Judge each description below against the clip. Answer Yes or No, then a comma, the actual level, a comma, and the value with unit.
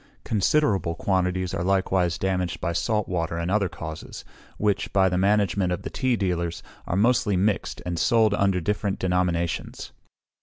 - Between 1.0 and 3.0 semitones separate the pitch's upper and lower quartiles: Yes, average, 2.7 semitones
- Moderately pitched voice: No, very low, 95 Hz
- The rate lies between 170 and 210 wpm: No, average, 155 wpm